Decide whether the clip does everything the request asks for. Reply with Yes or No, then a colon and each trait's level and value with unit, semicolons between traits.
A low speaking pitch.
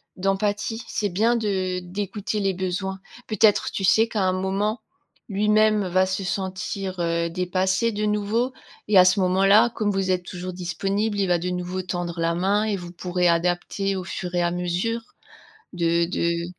No: high, 190 Hz